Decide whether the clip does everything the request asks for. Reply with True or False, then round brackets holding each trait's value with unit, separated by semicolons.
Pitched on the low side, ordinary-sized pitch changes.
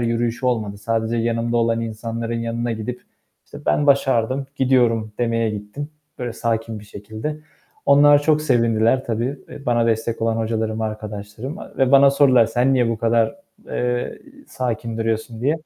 False (115 Hz; 2.1 semitones)